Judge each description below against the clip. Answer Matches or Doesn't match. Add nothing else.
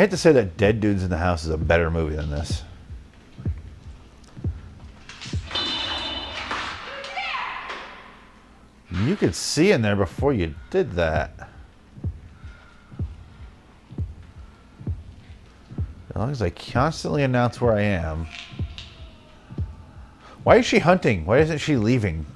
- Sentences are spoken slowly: Matches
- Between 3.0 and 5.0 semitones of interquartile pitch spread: Doesn't match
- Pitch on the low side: Matches